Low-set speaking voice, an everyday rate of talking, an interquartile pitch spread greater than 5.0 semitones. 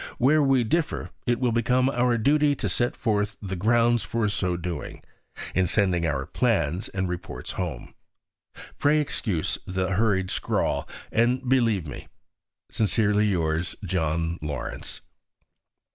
No: low, 105 Hz; slow, 130 wpm; wide, 5.5 semitones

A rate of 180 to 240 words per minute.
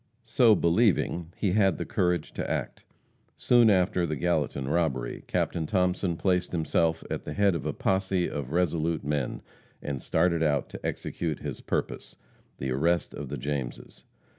No: average, 160 wpm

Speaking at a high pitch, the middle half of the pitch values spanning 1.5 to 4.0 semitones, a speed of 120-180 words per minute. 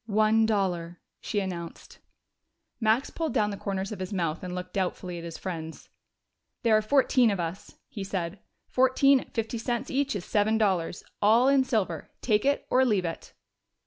No: high, 205 Hz; average, 4.4 semitones; average, 175 wpm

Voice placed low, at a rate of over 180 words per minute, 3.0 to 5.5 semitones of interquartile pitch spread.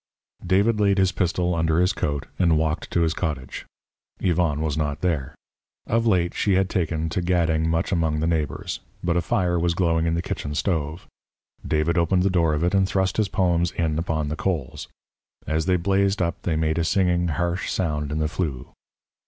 No: very low, 85 Hz; average, 195 wpm; narrow, 2.6 semitones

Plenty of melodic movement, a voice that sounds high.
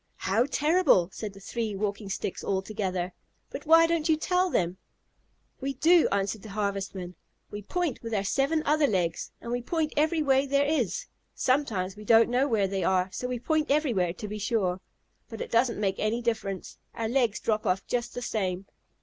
Yes: wide, 6.3 semitones; high, 225 Hz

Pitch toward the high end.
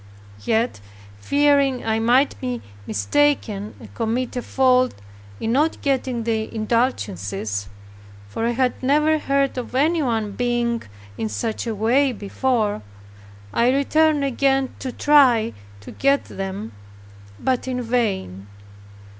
Yes: high, 245 Hz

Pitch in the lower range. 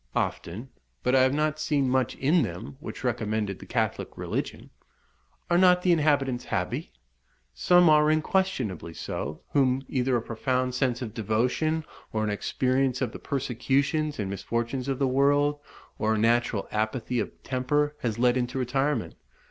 Yes: low, 130 Hz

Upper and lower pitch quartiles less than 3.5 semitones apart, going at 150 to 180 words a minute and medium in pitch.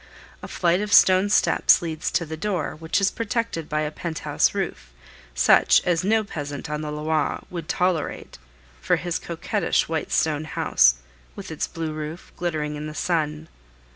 Yes: average, 2.9 semitones; average, 170 wpm; medium, 160 Hz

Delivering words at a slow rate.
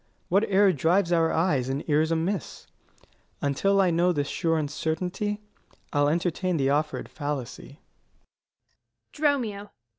Yes: slow, 115 wpm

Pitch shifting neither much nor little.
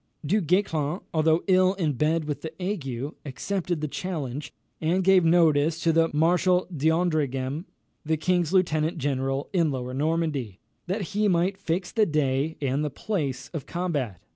Yes: average, 3.8 semitones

